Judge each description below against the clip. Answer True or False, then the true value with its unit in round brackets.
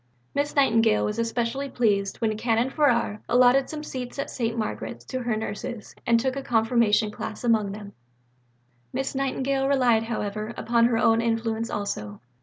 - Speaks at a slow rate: False (165 wpm)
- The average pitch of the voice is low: False (230 Hz)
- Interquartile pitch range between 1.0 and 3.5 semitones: True (2.9 semitones)